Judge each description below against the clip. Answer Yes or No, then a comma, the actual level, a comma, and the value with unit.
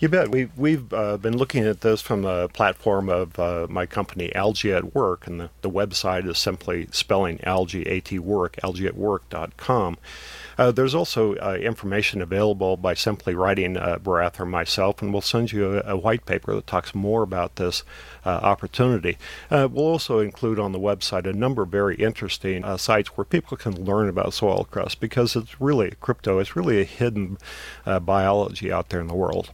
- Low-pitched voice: Yes, low, 100 Hz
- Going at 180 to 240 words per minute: Yes, average, 190 wpm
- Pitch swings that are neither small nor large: Yes, average, 3.2 semitones